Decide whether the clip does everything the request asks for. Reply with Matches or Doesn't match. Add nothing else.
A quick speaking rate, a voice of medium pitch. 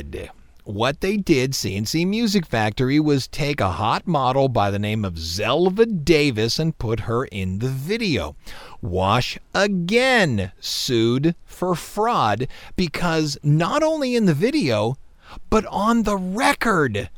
Doesn't match